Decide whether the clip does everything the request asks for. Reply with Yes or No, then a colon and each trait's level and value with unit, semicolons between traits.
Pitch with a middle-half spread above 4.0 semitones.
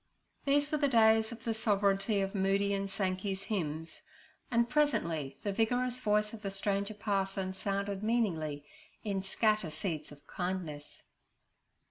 No: average, 2.7 semitones